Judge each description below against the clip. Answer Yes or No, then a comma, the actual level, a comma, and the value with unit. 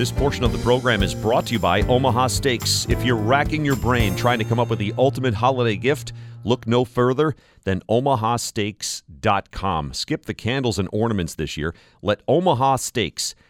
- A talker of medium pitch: No, low, 120 Hz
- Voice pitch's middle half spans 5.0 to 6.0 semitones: No, average, 3.0 semitones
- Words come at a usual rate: Yes, average, 180 wpm